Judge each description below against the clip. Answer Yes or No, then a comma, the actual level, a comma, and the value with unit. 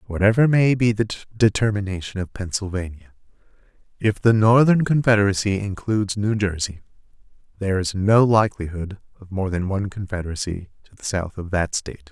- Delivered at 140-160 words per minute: Yes, average, 145 wpm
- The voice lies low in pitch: Yes, low, 100 Hz